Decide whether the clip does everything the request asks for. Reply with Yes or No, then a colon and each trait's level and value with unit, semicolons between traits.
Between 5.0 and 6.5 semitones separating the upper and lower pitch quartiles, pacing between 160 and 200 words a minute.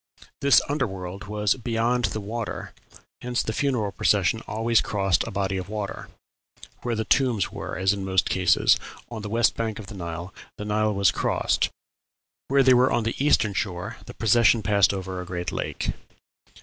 No: average, 3.2 semitones; average, 180 wpm